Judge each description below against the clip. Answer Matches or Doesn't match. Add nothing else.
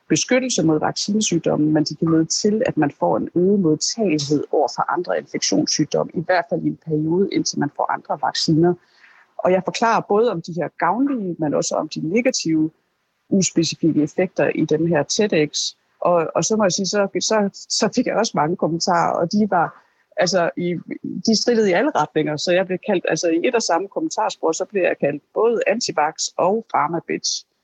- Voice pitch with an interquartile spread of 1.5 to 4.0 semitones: Doesn't match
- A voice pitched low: Doesn't match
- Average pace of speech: Matches